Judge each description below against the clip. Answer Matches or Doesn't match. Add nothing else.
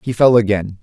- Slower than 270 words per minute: Matches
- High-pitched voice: Doesn't match